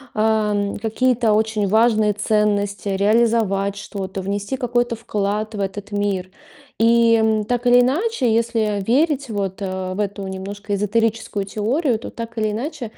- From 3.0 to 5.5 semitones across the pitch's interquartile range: No, narrow, 2.4 semitones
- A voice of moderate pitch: No, high, 215 Hz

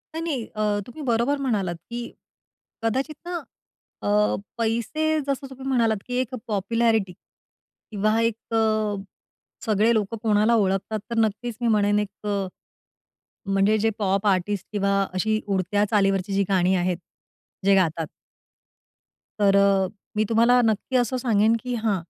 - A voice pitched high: Yes, high, 215 Hz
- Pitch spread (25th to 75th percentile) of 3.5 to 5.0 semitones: No, average, 2.9 semitones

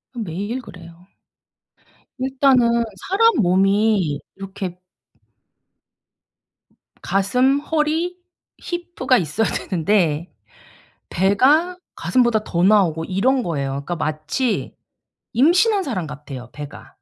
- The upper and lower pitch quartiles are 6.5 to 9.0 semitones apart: Yes, wide, 7.6 semitones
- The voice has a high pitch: Yes, high, 205 Hz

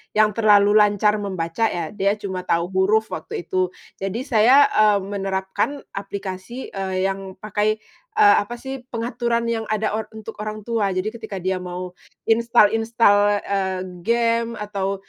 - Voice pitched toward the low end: No, high, 210 Hz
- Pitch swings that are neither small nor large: Yes, average, 3.0 semitones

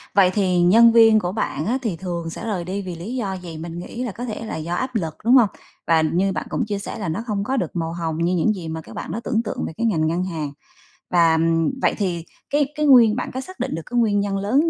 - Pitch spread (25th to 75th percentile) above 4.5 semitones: Yes, average, 5.2 semitones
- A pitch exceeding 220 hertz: No, high, 195 Hz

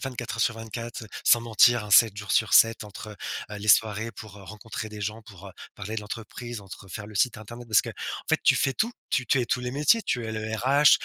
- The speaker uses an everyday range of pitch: No, narrow, 2.3 semitones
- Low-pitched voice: Yes, low, 110 Hz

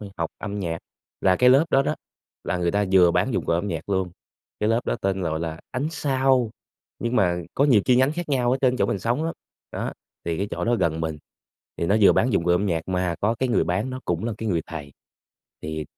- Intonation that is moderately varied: No, wide, 6.5 semitones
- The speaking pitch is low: Yes, low, 100 Hz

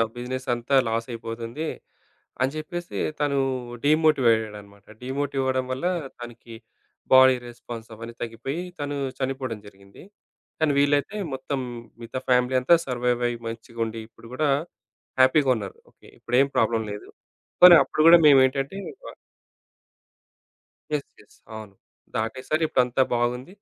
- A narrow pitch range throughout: No, average, 3.5 semitones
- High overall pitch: No, low, 125 Hz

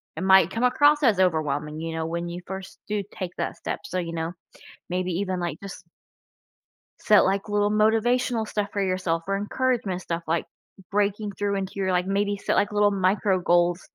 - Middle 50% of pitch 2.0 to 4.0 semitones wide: Yes, average, 2.9 semitones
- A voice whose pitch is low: No, high, 190 Hz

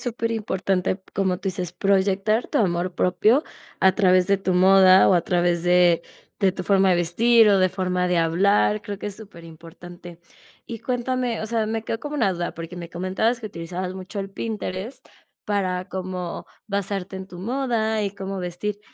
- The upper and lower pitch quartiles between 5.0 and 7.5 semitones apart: No, average, 2.9 semitones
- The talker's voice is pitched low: No, high, 190 Hz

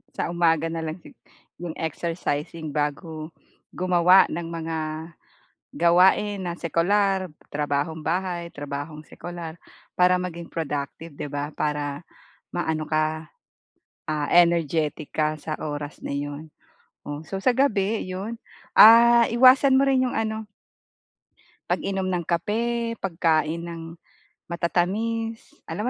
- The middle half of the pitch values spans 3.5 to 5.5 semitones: Yes, average, 3.9 semitones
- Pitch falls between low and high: Yes, medium, 170 Hz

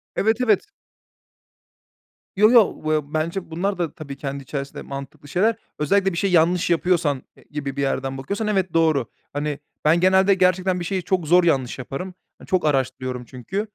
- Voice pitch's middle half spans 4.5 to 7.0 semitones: Yes, average, 5.2 semitones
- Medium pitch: Yes, medium, 165 Hz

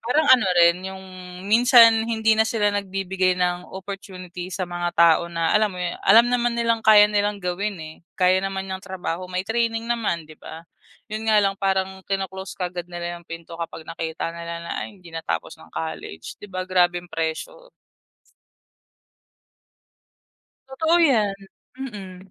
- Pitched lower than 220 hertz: Yes, high, 190 Hz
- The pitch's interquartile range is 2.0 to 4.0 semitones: Yes, average, 3.6 semitones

